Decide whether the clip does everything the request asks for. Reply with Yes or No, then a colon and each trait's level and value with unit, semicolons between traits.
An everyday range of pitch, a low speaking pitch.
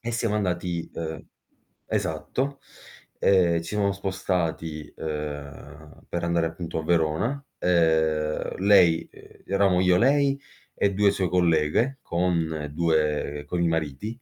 Yes: average, 3.8 semitones; very low, 85 Hz